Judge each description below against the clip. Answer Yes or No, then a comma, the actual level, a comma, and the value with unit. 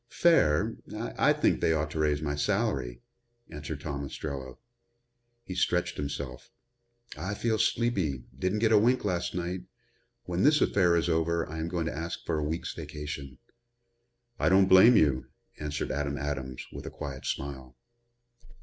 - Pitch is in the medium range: No, very low, 80 Hz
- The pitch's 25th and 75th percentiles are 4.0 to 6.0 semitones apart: Yes, average, 4.5 semitones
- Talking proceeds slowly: No, average, 160 wpm